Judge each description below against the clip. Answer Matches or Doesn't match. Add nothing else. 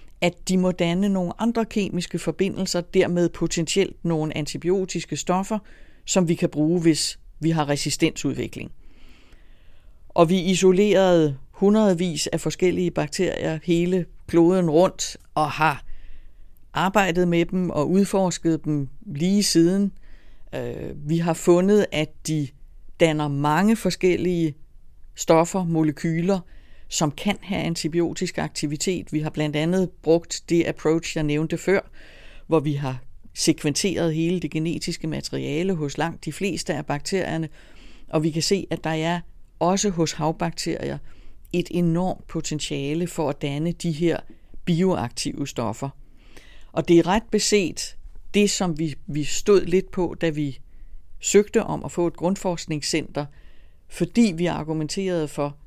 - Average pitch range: Matches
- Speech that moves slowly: Matches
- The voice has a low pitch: Doesn't match